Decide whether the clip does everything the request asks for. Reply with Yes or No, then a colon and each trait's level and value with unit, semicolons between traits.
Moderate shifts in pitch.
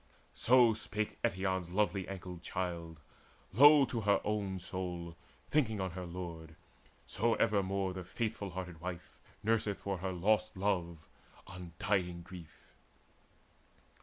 Yes: average, 3.1 semitones